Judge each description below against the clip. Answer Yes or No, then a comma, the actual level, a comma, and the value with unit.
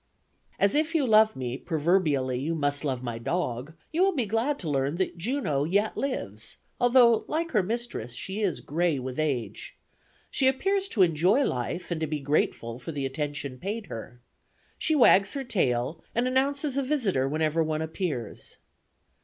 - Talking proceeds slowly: No, average, 170 wpm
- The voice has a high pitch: No, medium, 170 Hz